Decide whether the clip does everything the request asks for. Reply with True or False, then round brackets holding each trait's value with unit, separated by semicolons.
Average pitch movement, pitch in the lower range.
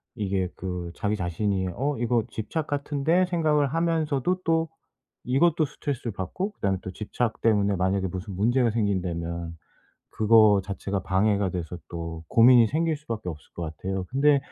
False (7.3 semitones; 110 Hz)